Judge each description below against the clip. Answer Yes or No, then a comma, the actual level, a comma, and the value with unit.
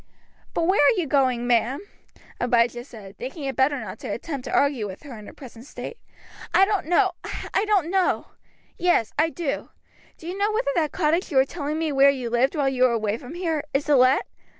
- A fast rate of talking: Yes, fast, 220 wpm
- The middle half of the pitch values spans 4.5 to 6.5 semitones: Yes, average, 5.2 semitones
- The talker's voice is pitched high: Yes, very high, 280 Hz